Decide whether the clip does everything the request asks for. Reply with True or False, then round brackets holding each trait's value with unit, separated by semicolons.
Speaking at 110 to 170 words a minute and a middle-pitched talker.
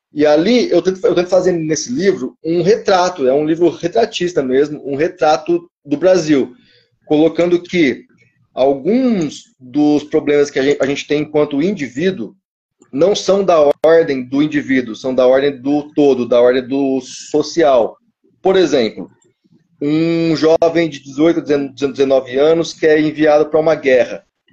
True (145 wpm; 155 Hz)